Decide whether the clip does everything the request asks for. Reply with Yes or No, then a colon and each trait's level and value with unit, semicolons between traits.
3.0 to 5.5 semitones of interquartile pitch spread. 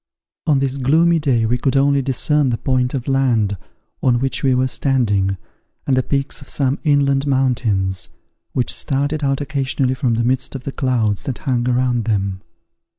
No: narrow, 2.4 semitones